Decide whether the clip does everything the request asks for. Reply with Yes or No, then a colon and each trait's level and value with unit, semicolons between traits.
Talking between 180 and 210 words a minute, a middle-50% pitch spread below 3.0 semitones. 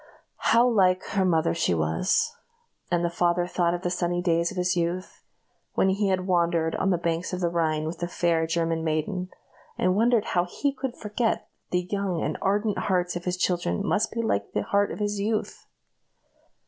Yes: average, 200 wpm; narrow, 2.6 semitones